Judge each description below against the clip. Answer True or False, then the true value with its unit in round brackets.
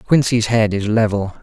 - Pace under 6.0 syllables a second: True (4.7 syllables/s)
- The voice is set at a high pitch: False (110 Hz)